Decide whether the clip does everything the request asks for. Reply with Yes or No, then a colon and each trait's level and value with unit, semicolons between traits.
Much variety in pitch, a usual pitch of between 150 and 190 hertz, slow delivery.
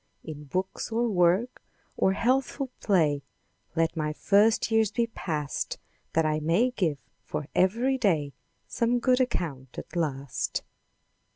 Yes: wide, 7.3 semitones; medium, 185 Hz; slow, 130 wpm